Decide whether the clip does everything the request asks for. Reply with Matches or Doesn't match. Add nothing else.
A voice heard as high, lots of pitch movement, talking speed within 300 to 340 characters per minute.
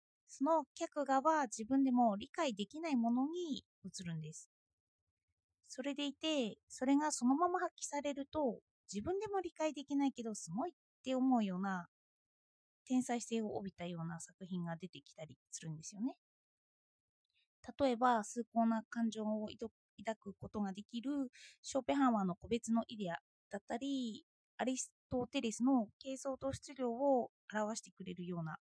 Matches